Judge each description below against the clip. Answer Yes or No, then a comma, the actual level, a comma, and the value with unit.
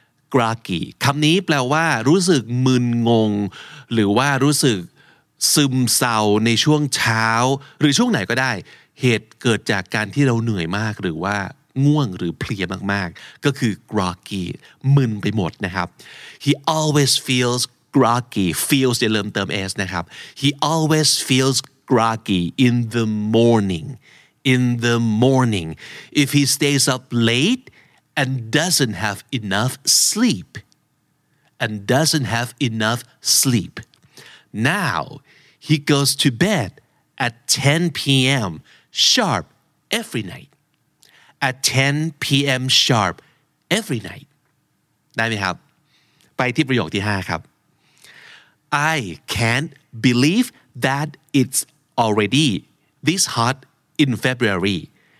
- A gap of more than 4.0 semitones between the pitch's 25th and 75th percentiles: Yes, average, 4.4 semitones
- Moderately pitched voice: No, low, 130 Hz